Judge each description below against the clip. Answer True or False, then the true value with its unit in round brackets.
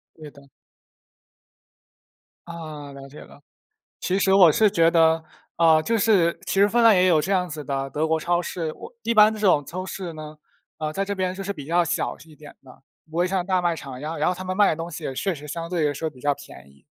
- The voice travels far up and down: False (3.6 semitones)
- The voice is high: False (165 Hz)